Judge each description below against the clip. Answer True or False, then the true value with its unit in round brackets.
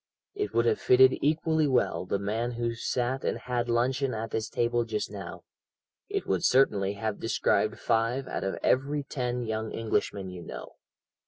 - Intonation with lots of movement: False (3.5 semitones)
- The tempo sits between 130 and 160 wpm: False (170 wpm)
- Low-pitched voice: True (120 Hz)